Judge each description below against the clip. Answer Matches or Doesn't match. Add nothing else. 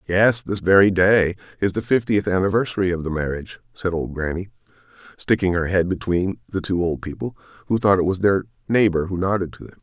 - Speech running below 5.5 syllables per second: Doesn't match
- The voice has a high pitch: Doesn't match